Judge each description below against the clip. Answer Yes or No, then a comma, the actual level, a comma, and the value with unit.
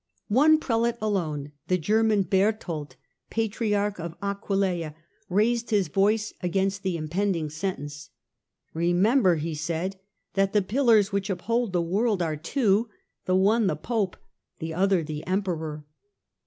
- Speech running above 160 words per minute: No, average, 140 wpm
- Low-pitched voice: No, high, 195 Hz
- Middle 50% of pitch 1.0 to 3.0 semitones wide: No, average, 4.2 semitones